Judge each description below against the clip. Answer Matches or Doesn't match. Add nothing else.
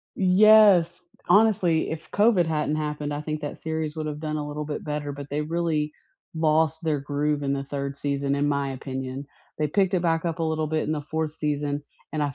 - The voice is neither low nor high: Matches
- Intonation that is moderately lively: Doesn't match